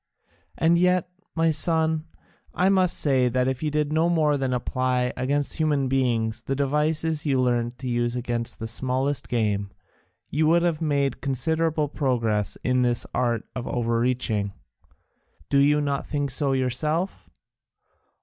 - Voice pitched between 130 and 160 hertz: Yes, low, 135 Hz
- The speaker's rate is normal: Yes, average, 150 wpm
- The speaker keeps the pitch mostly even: No, average, 3.9 semitones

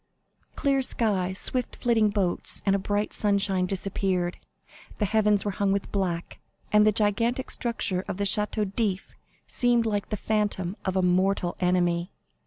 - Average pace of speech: Yes, average, 150 wpm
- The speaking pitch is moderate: No, high, 200 Hz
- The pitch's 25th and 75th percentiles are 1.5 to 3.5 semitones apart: Yes, narrow, 2.4 semitones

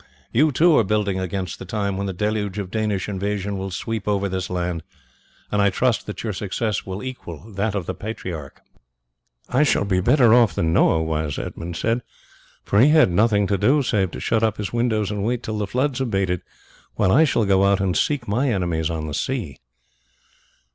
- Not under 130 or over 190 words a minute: No, average, 200 wpm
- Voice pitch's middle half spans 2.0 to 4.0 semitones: Yes, average, 3.4 semitones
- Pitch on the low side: Yes, low, 100 Hz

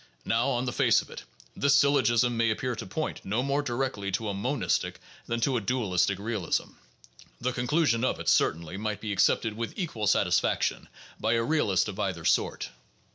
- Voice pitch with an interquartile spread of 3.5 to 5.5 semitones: Yes, average, 3.9 semitones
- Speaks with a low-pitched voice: Yes, low, 115 Hz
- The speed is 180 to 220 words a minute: Yes, average, 185 wpm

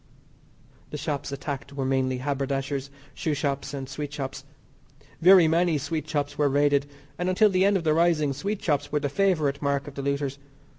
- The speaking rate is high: No, average, 185 wpm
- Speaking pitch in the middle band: Yes, medium, 145 Hz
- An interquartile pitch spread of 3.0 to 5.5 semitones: No, narrow, 2.5 semitones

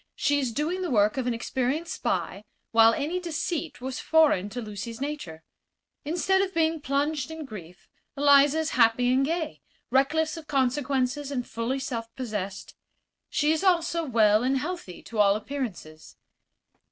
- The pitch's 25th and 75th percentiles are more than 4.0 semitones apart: Yes, wide, 5.5 semitones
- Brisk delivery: No, average, 155 wpm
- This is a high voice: Yes, very high, 270 Hz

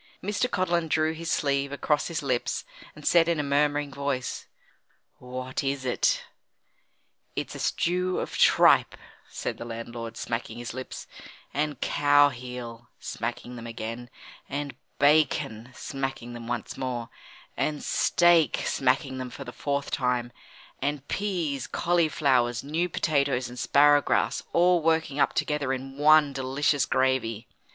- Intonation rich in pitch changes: No, average, 3.4 semitones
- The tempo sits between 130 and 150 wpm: Yes, average, 140 wpm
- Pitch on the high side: No, medium, 140 Hz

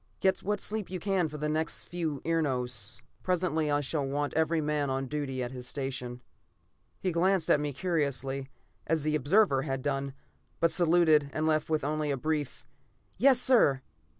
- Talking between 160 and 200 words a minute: Yes, average, 175 wpm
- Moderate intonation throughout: Yes, average, 3.5 semitones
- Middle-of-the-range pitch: Yes, medium, 150 Hz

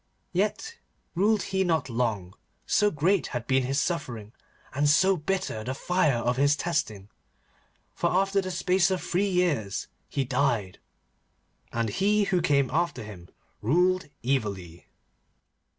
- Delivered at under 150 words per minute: Yes, slow, 135 wpm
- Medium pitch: Yes, medium, 150 Hz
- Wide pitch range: Yes, wide, 7.6 semitones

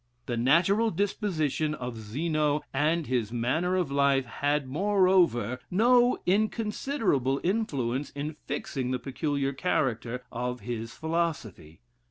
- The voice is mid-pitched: Yes, medium, 145 Hz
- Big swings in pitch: Yes, wide, 6.2 semitones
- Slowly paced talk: Yes, slow, 115 wpm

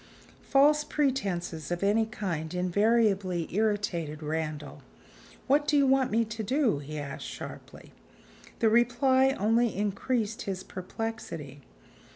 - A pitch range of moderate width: No, wide, 5.8 semitones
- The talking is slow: Yes, slow, 120 wpm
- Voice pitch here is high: Yes, high, 210 Hz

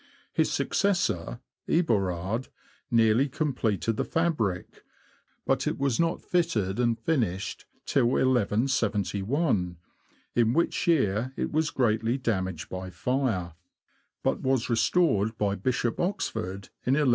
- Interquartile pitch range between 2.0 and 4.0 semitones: No, wide, 5.5 semitones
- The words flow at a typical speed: No, slow, 115 wpm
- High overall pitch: No, low, 115 Hz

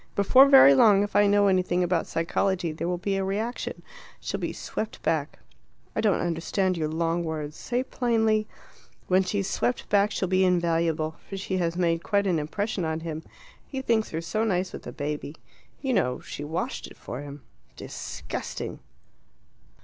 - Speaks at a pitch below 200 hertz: Yes, medium, 185 Hz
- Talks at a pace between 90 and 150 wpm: No, average, 180 wpm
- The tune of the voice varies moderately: Yes, average, 3.8 semitones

